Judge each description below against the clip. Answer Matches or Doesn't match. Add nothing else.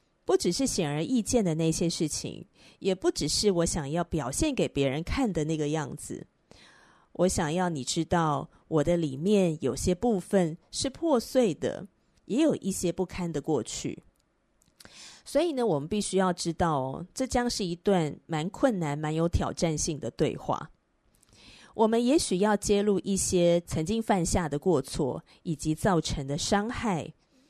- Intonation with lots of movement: Doesn't match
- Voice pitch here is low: Doesn't match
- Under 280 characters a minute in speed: Matches